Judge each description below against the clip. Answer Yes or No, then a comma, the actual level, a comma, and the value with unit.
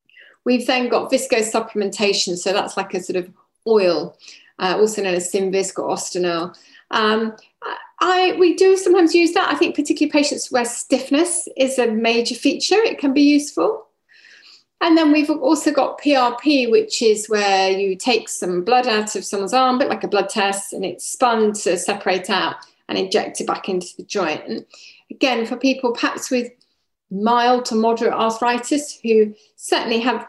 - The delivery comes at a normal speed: Yes, average, 170 wpm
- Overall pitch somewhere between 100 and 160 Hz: No, high, 240 Hz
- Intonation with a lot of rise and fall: Yes, wide, 6.0 semitones